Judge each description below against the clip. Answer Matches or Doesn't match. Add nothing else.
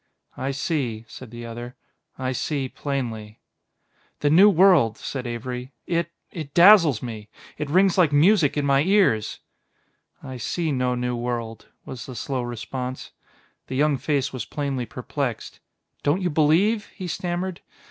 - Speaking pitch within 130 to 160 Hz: Matches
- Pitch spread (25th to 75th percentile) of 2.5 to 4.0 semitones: Doesn't match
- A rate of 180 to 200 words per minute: Doesn't match